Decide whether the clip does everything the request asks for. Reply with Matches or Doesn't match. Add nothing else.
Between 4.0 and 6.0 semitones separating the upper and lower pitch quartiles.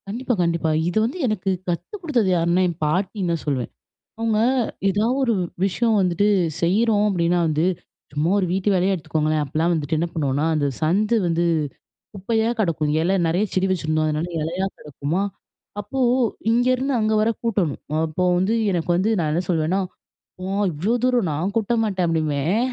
Matches